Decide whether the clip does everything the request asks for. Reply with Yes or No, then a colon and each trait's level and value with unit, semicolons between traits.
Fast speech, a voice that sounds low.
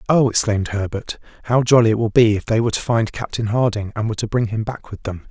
Yes: fast, 260 wpm; low, 110 Hz